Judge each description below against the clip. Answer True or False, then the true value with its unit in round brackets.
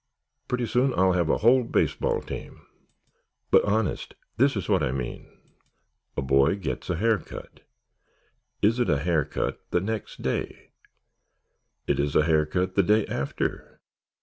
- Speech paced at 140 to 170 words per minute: True (155 wpm)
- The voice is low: True (95 Hz)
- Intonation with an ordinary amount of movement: False (6.6 semitones)